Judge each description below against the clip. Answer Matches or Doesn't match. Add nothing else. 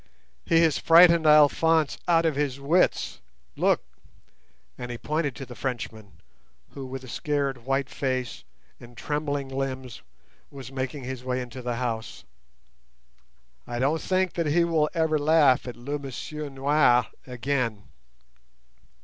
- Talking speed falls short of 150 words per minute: Matches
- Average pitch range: Matches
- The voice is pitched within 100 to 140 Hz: Matches